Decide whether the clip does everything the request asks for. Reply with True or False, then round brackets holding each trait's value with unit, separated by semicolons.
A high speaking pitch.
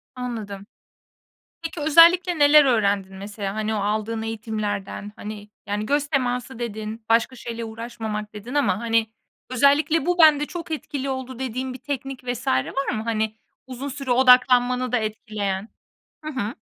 True (240 Hz)